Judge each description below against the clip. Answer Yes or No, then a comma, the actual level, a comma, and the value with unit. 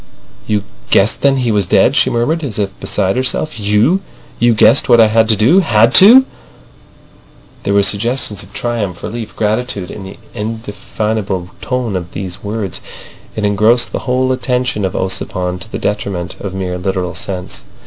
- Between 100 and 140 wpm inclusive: No, average, 170 wpm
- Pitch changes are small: No, average, 3.6 semitones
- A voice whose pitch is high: No, low, 105 Hz